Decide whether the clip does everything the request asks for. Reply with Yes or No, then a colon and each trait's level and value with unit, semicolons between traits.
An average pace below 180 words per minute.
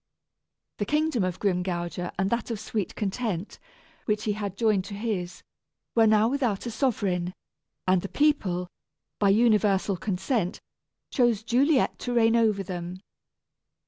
Yes: average, 140 wpm